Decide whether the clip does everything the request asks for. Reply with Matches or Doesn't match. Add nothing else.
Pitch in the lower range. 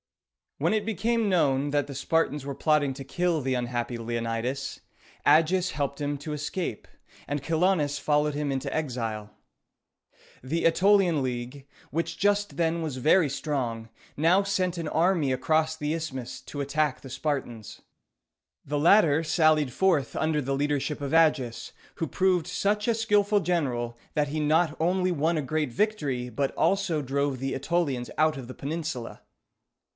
Doesn't match